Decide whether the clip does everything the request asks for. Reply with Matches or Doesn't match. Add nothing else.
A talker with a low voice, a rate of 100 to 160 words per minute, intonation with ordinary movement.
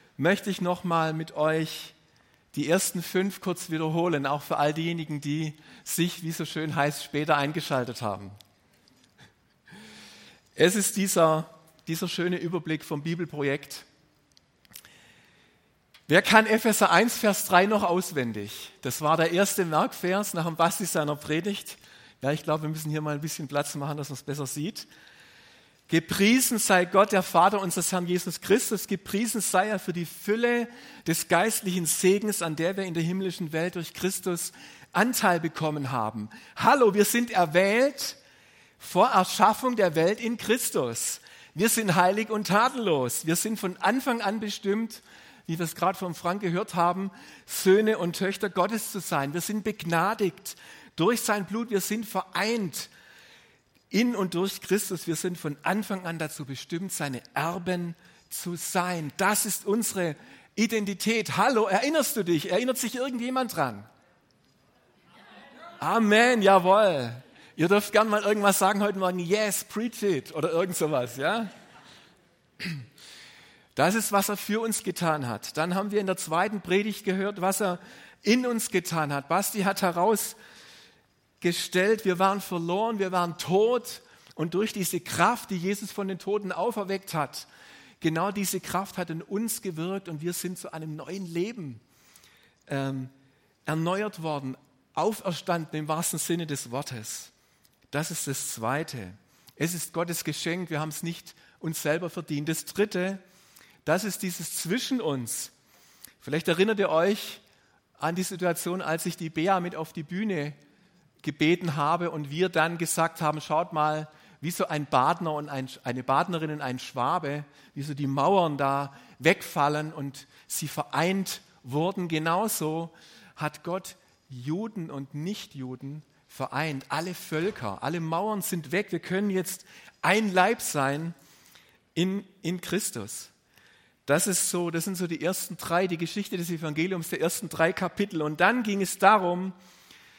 Doesn't match